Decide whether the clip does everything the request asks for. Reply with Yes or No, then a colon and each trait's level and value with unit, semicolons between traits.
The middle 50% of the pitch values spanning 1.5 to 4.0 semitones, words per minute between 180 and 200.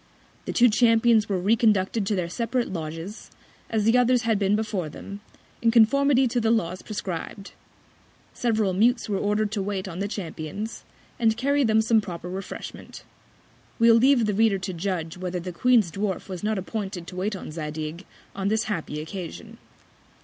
No: average, 3.6 semitones; average, 170 wpm